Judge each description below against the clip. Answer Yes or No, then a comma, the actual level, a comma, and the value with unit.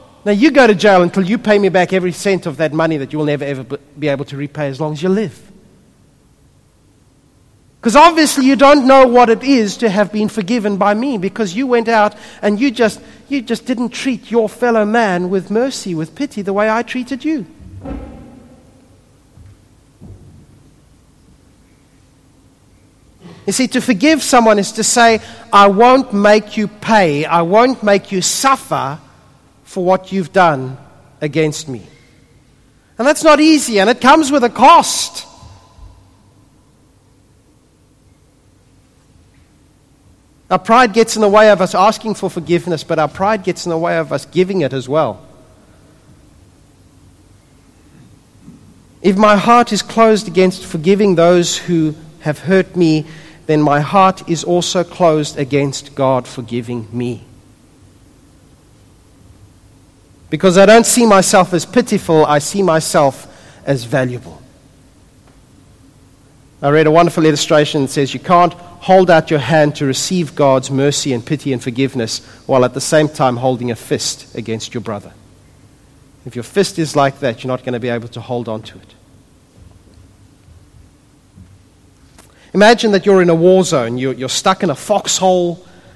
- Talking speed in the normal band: Yes, average, 155 wpm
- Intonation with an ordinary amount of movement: No, wide, 8.0 semitones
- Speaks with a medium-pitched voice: Yes, medium, 170 Hz